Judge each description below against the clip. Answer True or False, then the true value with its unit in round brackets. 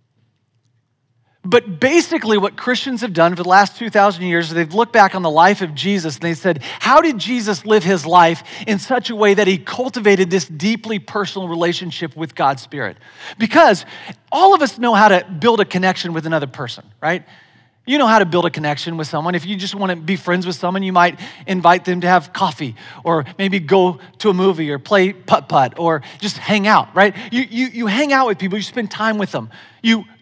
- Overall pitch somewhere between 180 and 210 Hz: True (190 Hz)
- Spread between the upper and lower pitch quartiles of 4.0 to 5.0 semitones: True (4.3 semitones)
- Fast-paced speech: True (215 wpm)